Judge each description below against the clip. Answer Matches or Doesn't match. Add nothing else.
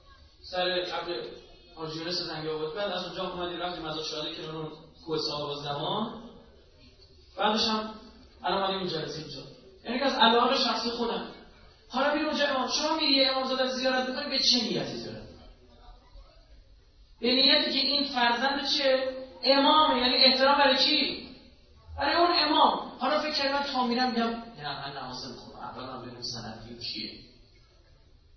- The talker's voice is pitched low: Doesn't match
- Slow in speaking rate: Doesn't match